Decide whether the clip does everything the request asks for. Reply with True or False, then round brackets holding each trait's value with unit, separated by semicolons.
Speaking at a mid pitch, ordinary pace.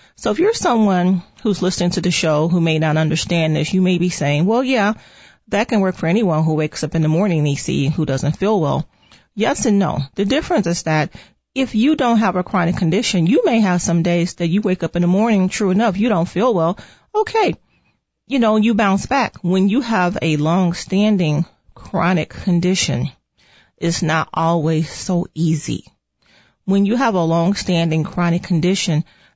True (180 Hz; 190 wpm)